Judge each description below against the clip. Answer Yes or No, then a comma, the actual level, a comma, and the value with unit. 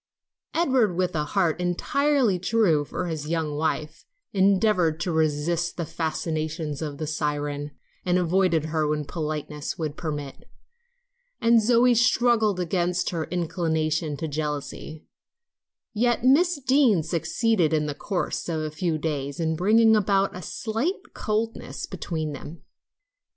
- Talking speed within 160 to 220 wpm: No, slow, 135 wpm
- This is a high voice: No, medium, 170 Hz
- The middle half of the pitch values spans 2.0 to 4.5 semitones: No, average, 5.3 semitones